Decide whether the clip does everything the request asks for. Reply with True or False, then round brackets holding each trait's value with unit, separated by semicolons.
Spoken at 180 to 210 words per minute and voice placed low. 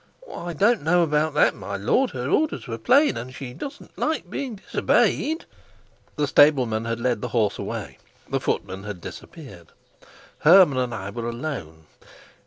False (160 wpm; 125 Hz)